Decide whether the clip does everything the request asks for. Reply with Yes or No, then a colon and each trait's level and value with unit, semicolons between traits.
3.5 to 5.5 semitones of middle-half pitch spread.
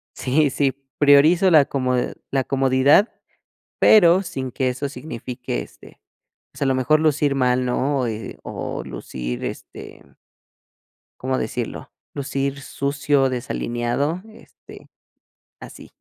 No: narrow, 2.4 semitones